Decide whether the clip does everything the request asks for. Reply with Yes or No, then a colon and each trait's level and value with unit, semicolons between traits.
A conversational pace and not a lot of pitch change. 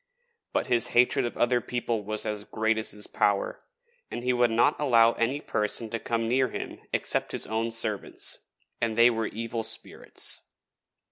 Yes: average, 175 wpm; narrow, 1.6 semitones